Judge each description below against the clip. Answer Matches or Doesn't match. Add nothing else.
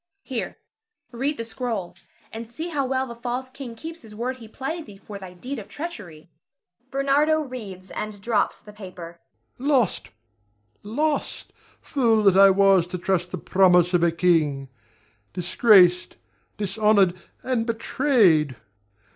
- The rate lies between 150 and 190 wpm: Doesn't match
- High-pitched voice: Matches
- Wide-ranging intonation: Matches